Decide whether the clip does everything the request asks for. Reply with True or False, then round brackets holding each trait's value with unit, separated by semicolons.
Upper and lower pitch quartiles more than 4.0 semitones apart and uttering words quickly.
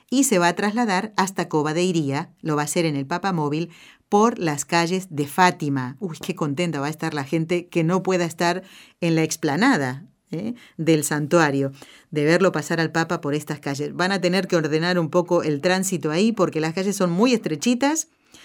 False (3.3 semitones; 200 wpm)